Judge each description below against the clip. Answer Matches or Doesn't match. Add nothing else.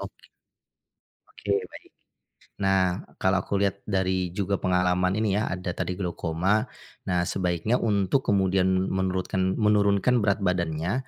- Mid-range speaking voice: Doesn't match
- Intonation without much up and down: Matches